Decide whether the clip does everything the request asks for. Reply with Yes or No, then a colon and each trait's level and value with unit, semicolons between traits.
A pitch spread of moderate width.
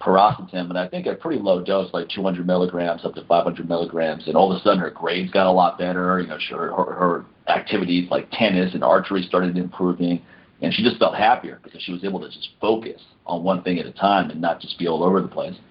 No: narrow, 1.0 semitones